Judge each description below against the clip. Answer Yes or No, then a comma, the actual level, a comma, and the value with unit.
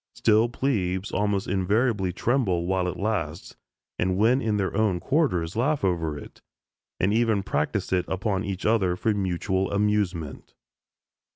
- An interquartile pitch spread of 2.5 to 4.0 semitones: Yes, average, 3.3 semitones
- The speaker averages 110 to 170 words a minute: Yes, average, 145 wpm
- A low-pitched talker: Yes, low, 100 Hz